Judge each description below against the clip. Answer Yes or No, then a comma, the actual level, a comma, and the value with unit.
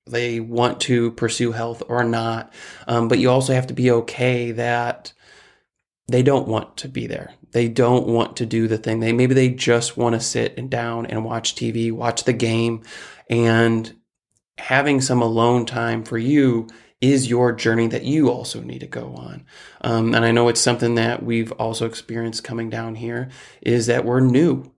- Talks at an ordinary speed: Yes, average, 190 wpm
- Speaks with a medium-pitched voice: No, low, 115 Hz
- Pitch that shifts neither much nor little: No, narrow, 1.2 semitones